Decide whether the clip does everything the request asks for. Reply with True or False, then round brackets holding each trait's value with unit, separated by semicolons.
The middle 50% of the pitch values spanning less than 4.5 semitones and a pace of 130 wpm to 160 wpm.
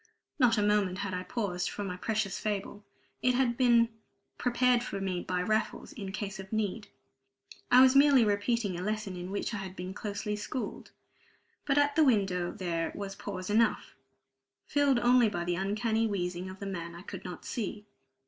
False (3.9 semitones; 185 wpm)